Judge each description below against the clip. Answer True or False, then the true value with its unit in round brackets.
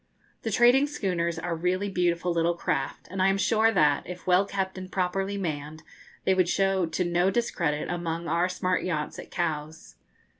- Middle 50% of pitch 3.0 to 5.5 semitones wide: False (2.5 semitones)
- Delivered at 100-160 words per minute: False (180 wpm)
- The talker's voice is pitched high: False (180 Hz)